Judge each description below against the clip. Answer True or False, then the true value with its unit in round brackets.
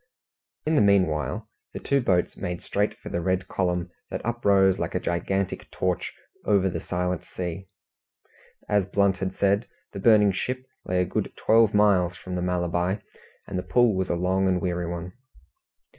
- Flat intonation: True (2.1 semitones)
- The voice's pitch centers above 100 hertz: False (95 Hz)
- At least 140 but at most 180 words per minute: True (175 wpm)